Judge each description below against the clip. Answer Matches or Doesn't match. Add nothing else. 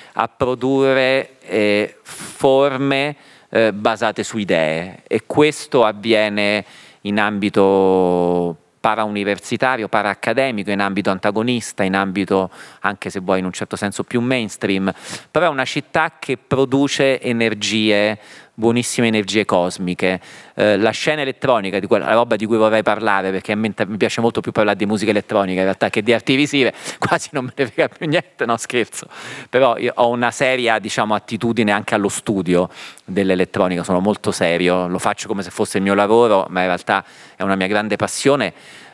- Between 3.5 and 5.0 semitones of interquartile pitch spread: Matches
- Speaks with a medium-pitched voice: Doesn't match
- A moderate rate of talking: Matches